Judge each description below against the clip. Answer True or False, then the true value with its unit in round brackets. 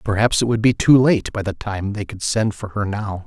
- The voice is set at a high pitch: False (105 Hz)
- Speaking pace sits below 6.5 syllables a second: True (5.1 syllables/s)